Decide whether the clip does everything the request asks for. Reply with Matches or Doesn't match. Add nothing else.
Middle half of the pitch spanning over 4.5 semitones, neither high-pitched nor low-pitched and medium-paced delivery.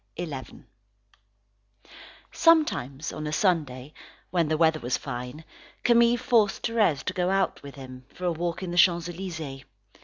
Matches